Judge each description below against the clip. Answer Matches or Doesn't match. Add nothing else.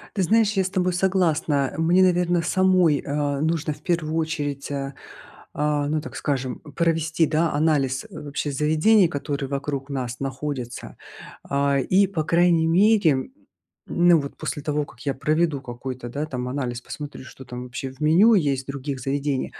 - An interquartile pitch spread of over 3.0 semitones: Matches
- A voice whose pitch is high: Doesn't match